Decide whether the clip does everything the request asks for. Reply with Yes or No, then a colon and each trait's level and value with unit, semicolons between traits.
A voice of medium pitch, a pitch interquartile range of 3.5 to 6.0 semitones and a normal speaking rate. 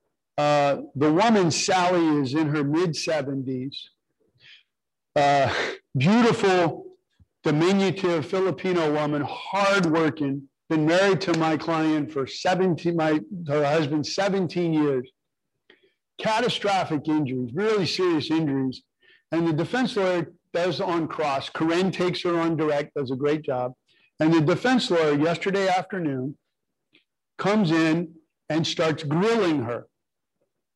No: medium, 165 Hz; average, 3.8 semitones; slow, 115 wpm